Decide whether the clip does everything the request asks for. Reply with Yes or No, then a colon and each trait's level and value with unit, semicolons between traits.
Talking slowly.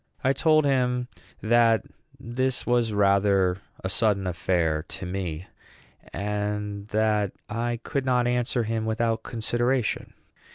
Yes: slow, 120 wpm